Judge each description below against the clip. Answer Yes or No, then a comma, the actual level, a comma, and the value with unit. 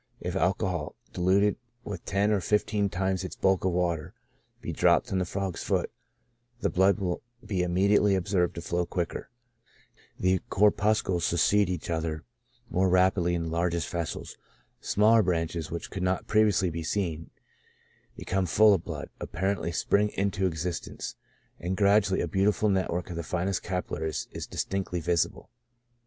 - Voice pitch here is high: No, very low, 95 Hz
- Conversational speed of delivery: Yes, average, 155 wpm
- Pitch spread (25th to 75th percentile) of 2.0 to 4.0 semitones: Yes, narrow, 2.5 semitones